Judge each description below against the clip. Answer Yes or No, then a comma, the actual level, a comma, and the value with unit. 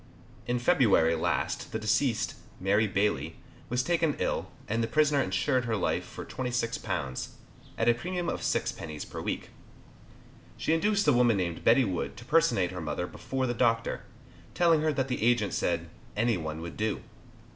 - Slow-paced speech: No, average, 170 wpm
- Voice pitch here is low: Yes, low, 115 Hz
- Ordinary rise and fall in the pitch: No, wide, 6.0 semitones